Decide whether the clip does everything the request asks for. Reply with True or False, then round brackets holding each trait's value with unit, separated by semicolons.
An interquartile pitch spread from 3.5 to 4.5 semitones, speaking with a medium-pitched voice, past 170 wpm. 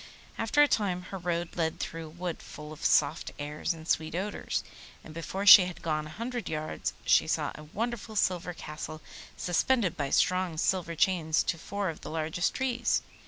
True (3.8 semitones; 175 Hz; 185 wpm)